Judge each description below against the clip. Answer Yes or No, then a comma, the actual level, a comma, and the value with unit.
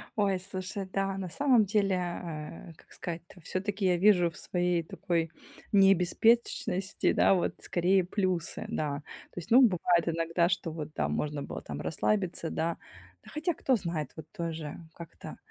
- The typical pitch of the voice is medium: Yes, medium, 180 Hz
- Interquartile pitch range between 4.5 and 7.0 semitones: No, average, 2.8 semitones